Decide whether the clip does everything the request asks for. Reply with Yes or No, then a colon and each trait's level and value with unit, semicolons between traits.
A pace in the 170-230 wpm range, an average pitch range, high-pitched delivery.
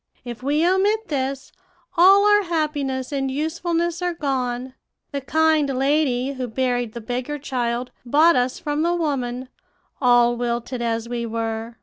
No: average, 145 wpm; average, 4.4 semitones; very high, 265 Hz